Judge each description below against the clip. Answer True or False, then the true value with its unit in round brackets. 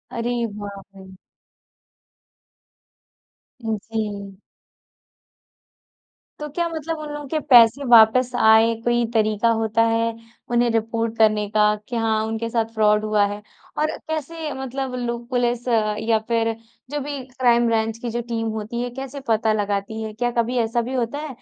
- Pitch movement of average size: False (2.1 semitones)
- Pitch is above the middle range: True (230 Hz)